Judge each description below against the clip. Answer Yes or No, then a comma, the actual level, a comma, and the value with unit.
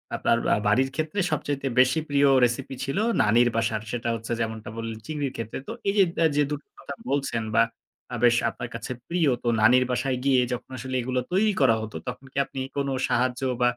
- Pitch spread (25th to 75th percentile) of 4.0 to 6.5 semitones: No, average, 3.1 semitones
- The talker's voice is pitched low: Yes, low, 125 Hz